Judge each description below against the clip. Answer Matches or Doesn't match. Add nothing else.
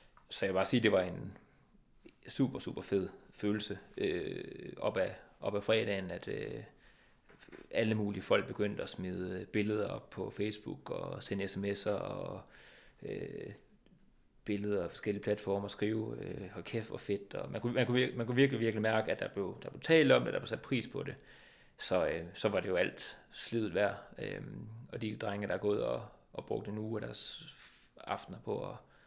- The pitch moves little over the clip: Matches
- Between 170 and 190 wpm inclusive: Doesn't match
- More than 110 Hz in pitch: Doesn't match